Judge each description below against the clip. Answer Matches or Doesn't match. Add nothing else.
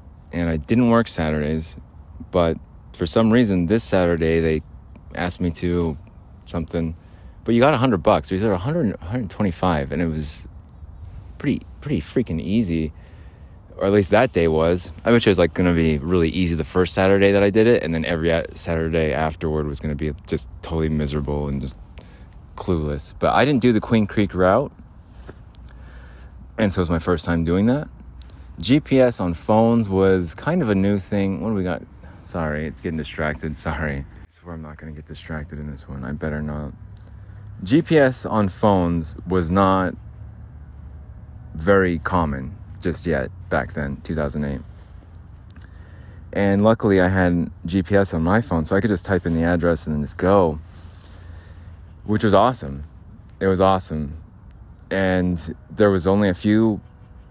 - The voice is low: Matches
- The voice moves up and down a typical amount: Matches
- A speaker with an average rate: Matches